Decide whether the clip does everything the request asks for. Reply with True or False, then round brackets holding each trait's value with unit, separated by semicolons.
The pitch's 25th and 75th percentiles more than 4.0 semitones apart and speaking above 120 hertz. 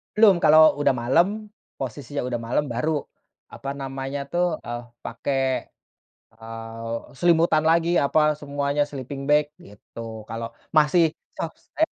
True (4.8 semitones; 140 Hz)